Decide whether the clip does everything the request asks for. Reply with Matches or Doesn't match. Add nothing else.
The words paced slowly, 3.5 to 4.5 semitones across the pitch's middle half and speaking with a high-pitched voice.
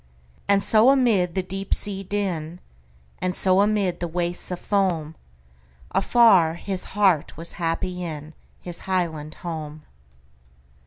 Doesn't match